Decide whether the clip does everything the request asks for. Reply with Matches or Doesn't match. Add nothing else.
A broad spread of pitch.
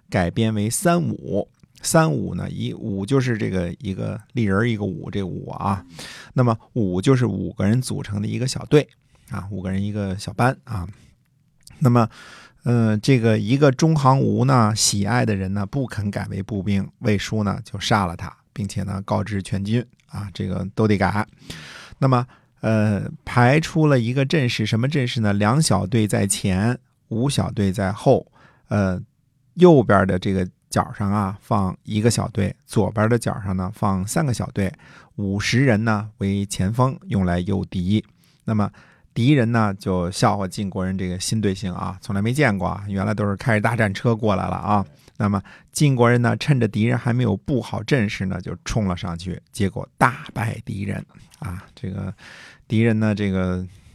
Doesn't match